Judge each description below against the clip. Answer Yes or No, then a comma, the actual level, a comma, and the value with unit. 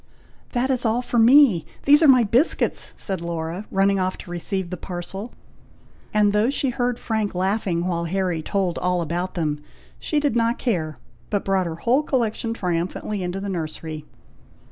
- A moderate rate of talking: Yes, average, 170 wpm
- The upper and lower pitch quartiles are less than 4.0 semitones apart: No, average, 5.1 semitones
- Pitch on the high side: Yes, high, 195 Hz